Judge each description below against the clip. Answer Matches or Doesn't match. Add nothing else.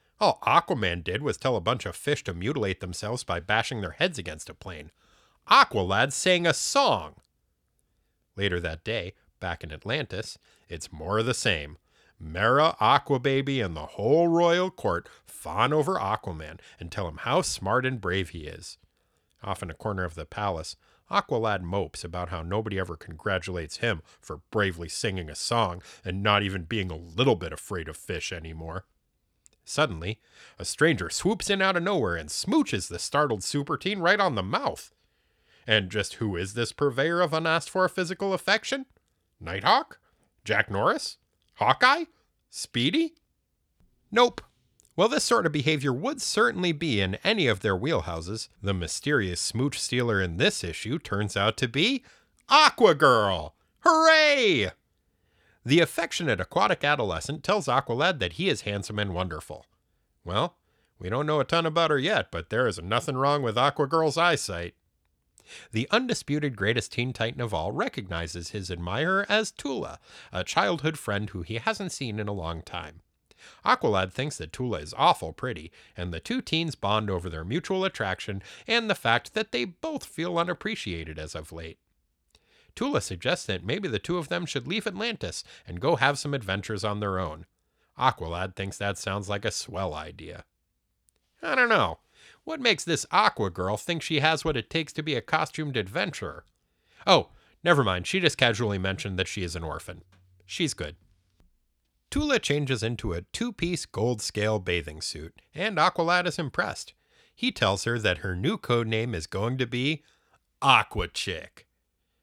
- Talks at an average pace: Matches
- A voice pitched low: Matches